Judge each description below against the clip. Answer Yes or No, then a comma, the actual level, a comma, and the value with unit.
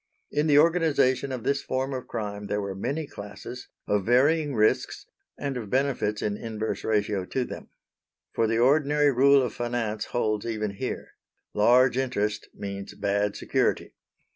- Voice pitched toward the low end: Yes, low, 120 Hz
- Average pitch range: Yes, average, 4.7 semitones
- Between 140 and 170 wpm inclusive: Yes, average, 155 wpm